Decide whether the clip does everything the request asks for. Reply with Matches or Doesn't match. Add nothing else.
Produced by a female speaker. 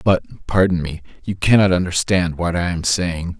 Doesn't match